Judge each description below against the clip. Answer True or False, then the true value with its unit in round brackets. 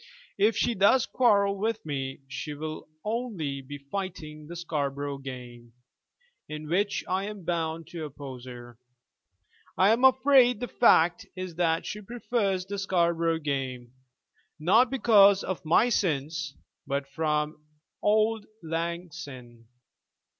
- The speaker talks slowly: True (130 wpm)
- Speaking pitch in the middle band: True (165 Hz)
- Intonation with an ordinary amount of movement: False (6.0 semitones)